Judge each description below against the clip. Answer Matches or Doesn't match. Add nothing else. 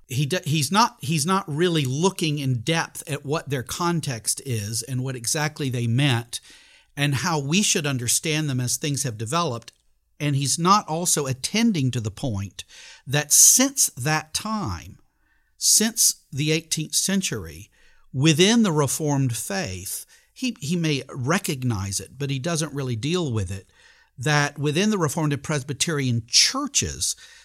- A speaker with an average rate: Matches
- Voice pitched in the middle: Matches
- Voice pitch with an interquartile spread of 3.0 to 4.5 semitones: Doesn't match